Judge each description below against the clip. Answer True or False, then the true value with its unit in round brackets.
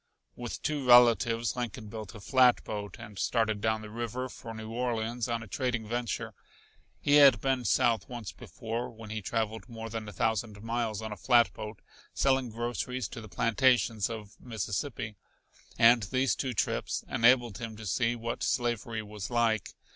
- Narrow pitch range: True (1.8 semitones)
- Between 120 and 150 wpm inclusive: False (165 wpm)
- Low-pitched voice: True (115 Hz)